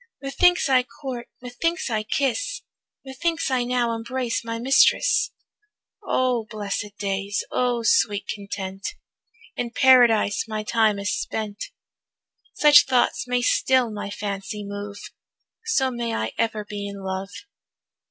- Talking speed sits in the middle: No, slow, 125 wpm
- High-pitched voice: Yes, high, 230 Hz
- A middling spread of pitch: Yes, average, 4.0 semitones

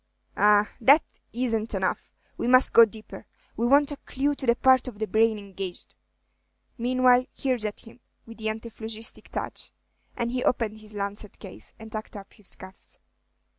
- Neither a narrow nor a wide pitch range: Yes, average, 3.0 semitones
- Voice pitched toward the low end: No, high, 225 Hz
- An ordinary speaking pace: Yes, average, 170 wpm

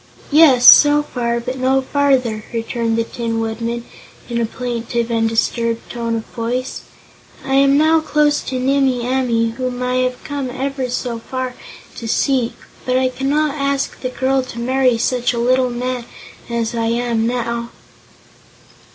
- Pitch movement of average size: No, narrow, 2.3 semitones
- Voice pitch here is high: Yes, very high, 250 Hz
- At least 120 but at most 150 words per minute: No, average, 160 wpm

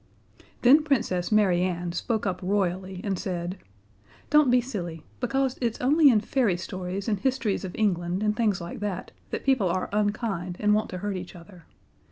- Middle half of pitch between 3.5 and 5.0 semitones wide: Yes, average, 4.3 semitones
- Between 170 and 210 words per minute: Yes, average, 180 wpm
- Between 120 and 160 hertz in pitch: No, high, 200 Hz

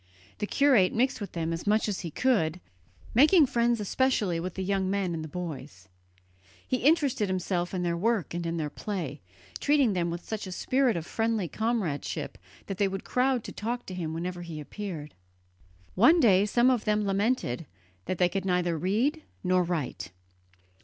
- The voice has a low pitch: No, high, 195 Hz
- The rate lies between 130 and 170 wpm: No, average, 180 wpm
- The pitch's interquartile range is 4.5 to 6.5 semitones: Yes, average, 5.3 semitones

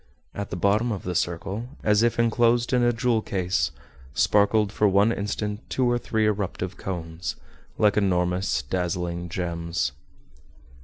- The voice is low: Yes, low, 100 Hz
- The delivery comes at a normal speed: Yes, average, 145 wpm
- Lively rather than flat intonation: No, average, 3.9 semitones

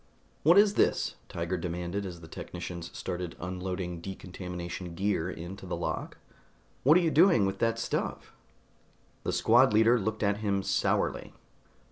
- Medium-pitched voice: No, very low, 95 Hz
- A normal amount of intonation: Yes, average, 4.0 semitones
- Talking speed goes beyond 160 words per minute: No, average, 145 wpm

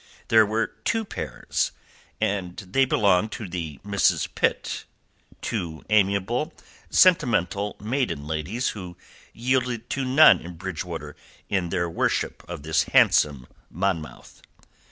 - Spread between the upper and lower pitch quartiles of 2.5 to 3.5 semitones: No, average, 5.3 semitones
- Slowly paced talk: Yes, slow, 115 wpm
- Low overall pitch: Yes, low, 100 Hz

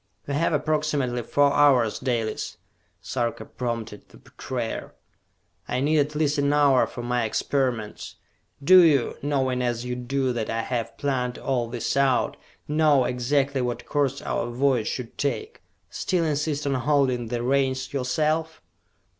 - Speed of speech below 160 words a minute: Yes, average, 145 wpm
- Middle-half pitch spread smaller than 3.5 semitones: Yes, average, 2.9 semitones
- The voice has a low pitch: Yes, low, 130 Hz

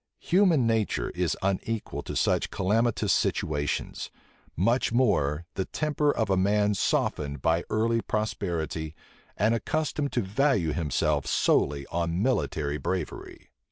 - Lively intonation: Yes, wide, 6.4 semitones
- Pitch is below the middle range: Yes, low, 100 Hz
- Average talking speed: No, slow, 120 wpm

